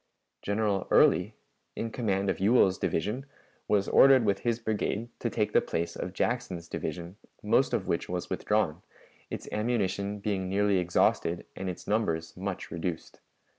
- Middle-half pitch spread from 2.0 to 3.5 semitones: Yes, average, 3.1 semitones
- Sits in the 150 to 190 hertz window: No, low, 100 Hz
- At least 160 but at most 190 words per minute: No, average, 150 wpm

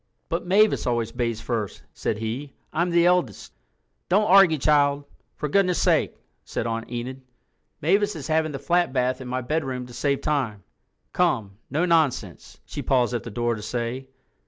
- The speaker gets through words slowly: No, average, 165 wpm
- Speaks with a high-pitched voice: No, low, 135 Hz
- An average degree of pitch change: No, wide, 5.8 semitones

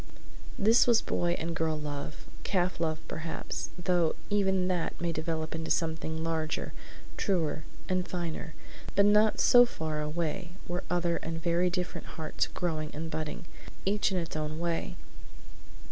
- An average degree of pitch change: No, narrow, 2.3 semitones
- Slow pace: No, average, 150 wpm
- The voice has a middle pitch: Yes, medium, 170 Hz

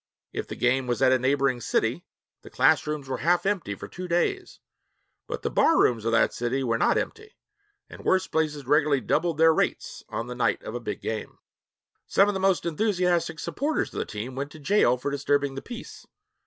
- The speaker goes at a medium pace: No, fast, 210 wpm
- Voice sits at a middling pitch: Yes, medium, 145 Hz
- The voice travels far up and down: Yes, wide, 5.9 semitones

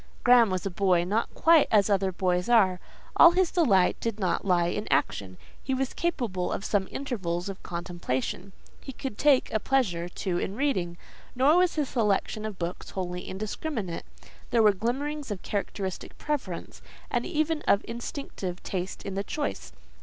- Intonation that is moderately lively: No, wide, 6.4 semitones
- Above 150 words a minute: Yes, average, 170 wpm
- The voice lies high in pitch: Yes, high, 200 Hz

